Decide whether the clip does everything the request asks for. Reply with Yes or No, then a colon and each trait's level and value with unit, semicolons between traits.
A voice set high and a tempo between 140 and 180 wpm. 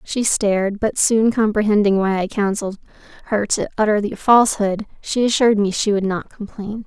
Yes: high, 210 Hz; average, 175 wpm